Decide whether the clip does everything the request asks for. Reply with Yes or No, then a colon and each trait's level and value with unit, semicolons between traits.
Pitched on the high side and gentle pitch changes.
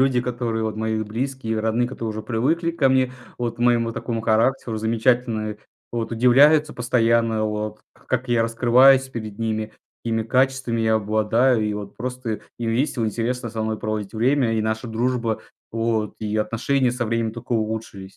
No: low, 115 Hz; narrow, 2.2 semitones